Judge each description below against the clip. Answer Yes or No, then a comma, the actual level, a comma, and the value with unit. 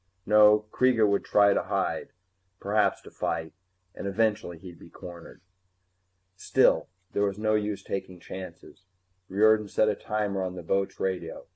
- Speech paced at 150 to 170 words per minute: Yes, average, 155 wpm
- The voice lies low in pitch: Yes, low, 100 Hz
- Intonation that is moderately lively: No, narrow, 2.3 semitones